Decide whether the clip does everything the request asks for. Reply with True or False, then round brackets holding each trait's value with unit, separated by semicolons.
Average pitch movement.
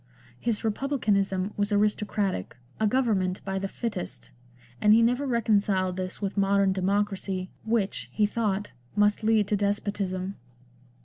False (2.0 semitones)